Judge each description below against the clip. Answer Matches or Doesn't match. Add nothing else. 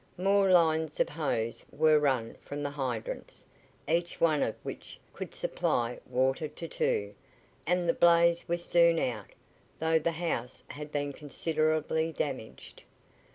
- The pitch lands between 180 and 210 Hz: Doesn't match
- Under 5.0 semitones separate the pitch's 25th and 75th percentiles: Matches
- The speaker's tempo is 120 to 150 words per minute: Matches